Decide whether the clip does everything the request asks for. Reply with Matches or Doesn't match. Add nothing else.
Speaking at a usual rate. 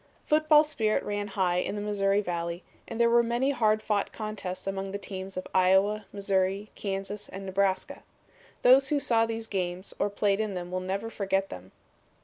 Matches